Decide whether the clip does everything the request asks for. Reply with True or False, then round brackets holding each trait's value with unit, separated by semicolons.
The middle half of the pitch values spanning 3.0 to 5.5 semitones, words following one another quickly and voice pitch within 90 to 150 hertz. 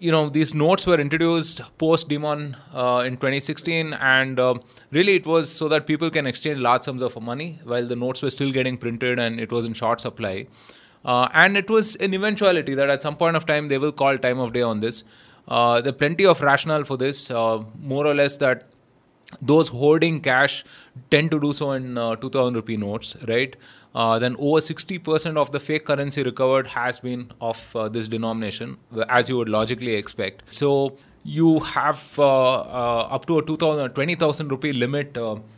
False (4.1 semitones; 195 wpm; 135 Hz)